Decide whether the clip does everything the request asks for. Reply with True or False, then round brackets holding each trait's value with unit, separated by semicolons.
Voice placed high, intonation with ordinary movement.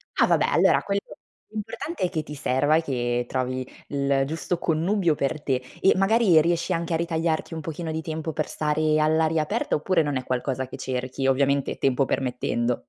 False (155 Hz; 3.6 semitones)